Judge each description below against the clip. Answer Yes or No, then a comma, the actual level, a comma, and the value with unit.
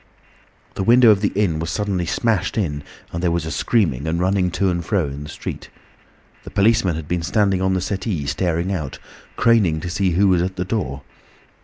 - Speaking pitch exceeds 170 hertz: No, very low, 90 Hz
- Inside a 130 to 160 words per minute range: No, fast, 205 wpm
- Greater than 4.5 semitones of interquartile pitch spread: No, average, 3.6 semitones